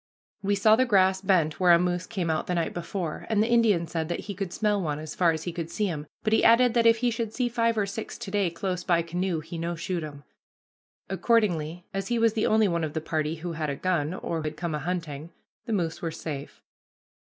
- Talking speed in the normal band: No, fast, 250 wpm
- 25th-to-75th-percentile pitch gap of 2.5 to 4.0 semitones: No, average, 4.5 semitones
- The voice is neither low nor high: Yes, medium, 180 Hz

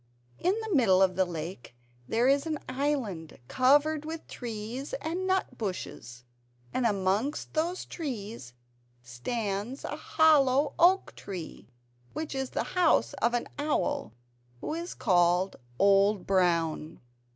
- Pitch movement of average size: No, wide, 8.3 semitones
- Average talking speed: No, slow, 130 wpm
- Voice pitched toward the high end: Yes, high, 240 Hz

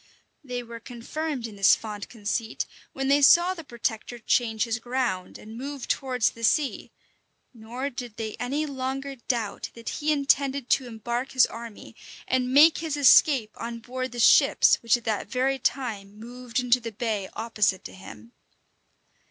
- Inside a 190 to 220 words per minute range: No, average, 165 wpm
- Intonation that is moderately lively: Yes, average, 3.2 semitones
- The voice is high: Yes, high, 245 Hz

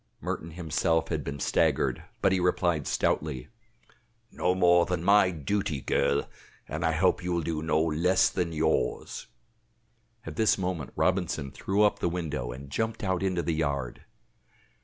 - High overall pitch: No, very low, 85 Hz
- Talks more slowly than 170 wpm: Yes, average, 160 wpm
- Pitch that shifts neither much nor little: Yes, average, 3.1 semitones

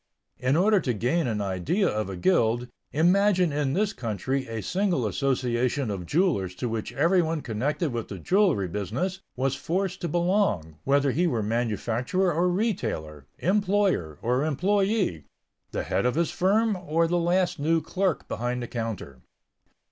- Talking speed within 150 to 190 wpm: Yes, average, 155 wpm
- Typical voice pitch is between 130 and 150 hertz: Yes, medium, 140 Hz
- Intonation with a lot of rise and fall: Yes, wide, 8.1 semitones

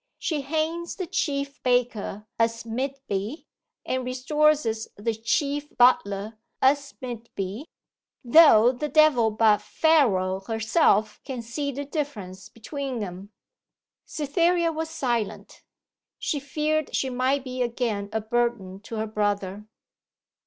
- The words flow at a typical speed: No, slow, 125 wpm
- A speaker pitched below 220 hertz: No, high, 245 Hz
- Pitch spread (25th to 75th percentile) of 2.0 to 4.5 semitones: No, average, 5.0 semitones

